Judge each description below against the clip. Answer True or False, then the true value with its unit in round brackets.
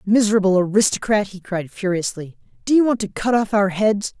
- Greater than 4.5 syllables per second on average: True (5.5 syllables/s)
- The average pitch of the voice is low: False (205 Hz)